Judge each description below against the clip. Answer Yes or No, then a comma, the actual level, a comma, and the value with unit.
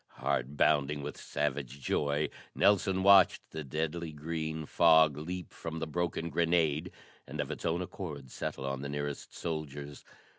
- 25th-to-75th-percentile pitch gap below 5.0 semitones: Yes, narrow, 2.6 semitones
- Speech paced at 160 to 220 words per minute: No, average, 150 wpm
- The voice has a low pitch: Yes, very low, 80 Hz